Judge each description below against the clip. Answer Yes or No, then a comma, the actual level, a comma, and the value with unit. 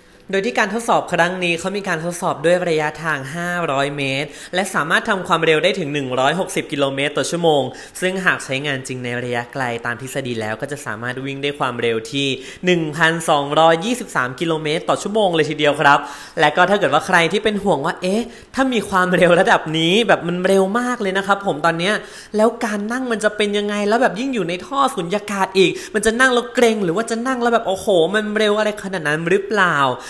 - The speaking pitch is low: No, medium, 175 Hz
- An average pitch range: No, wide, 6.0 semitones